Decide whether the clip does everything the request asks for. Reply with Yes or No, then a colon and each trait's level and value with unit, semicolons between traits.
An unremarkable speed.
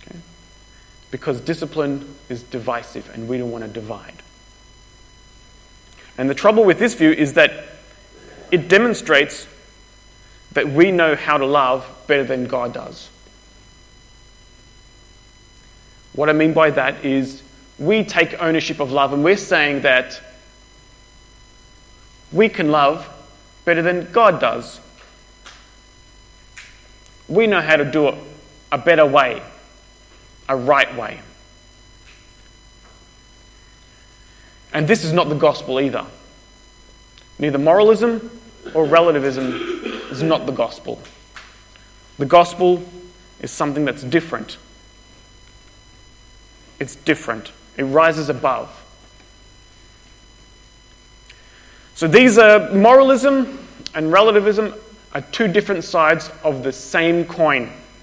No: slow, 110 wpm